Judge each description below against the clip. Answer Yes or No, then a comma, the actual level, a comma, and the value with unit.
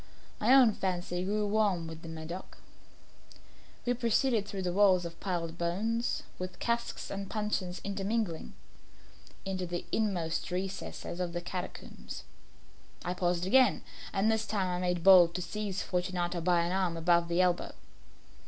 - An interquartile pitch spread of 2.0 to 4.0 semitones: Yes, average, 2.9 semitones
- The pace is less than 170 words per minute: Yes, average, 145 wpm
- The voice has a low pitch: No, medium, 185 Hz